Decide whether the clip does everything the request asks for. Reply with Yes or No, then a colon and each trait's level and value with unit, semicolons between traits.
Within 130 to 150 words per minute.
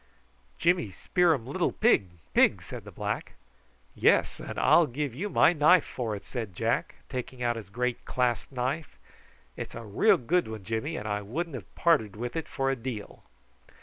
No: average, 180 wpm